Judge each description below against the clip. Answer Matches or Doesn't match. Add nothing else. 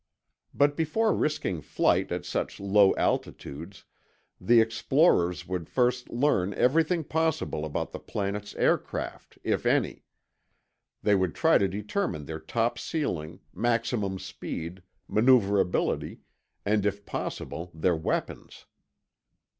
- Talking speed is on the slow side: Matches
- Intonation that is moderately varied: Doesn't match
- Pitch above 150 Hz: Doesn't match